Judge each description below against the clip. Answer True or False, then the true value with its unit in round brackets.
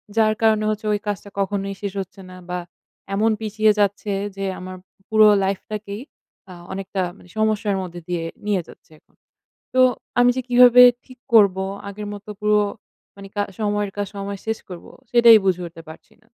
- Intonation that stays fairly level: True (1.9 semitones)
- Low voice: False (205 Hz)